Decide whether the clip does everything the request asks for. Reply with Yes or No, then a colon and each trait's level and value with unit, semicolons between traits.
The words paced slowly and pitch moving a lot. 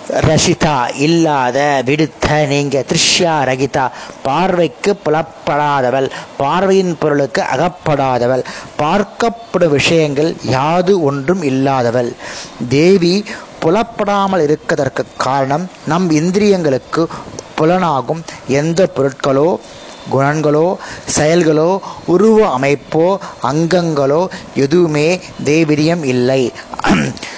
No: slow, 70 wpm; average, 4.3 semitones